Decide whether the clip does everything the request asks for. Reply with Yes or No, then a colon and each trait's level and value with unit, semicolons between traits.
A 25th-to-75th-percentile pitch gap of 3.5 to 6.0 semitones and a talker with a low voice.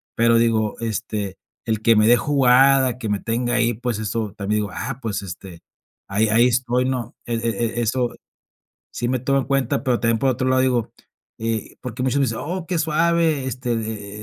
No: average, 2.8 semitones; low, 120 Hz